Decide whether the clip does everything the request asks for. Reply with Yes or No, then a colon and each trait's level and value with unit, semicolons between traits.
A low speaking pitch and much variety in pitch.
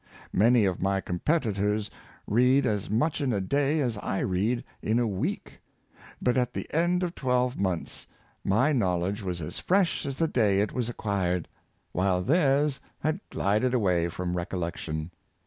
Yes: low, 110 Hz; wide, 5.9 semitones